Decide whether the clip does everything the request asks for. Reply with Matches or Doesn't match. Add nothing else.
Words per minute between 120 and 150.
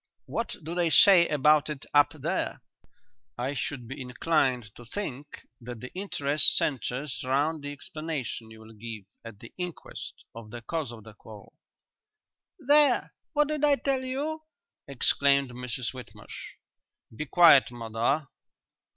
Matches